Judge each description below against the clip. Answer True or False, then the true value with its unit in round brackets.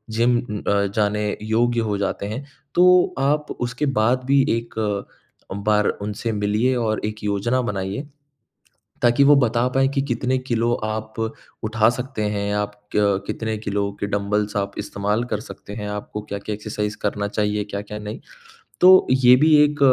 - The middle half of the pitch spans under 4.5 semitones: True (3.3 semitones)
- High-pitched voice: False (110 Hz)